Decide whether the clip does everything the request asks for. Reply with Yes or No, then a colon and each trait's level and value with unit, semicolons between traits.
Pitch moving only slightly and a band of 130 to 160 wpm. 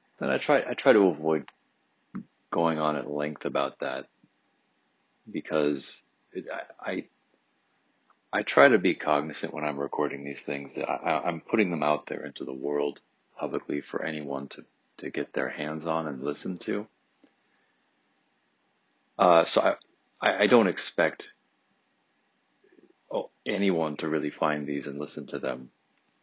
Yes: narrow, 1.6 semitones; average, 145 wpm